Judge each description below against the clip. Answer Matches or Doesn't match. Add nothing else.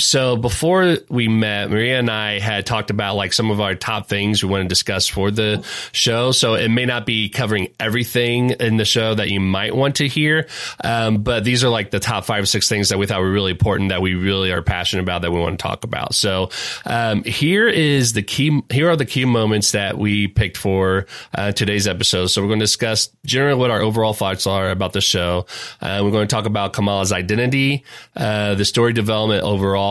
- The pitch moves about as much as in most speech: Matches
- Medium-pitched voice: Doesn't match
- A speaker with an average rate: Doesn't match